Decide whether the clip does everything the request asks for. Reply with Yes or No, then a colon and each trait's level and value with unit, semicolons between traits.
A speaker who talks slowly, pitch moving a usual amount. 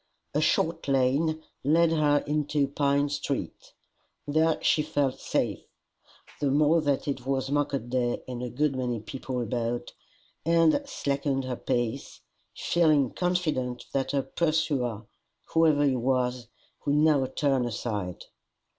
Yes: slow, 130 wpm; average, 3.3 semitones